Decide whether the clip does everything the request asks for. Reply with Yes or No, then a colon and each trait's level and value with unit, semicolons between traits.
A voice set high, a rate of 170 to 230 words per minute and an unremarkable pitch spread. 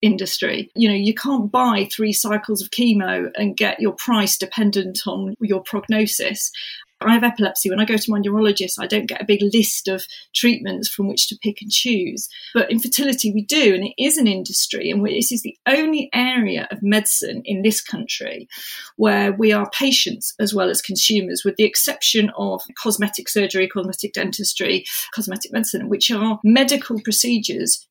No: high, 215 Hz; average, 180 wpm; narrow, 2.3 semitones